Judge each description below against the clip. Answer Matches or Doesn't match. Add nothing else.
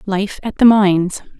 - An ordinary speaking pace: Matches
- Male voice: Doesn't match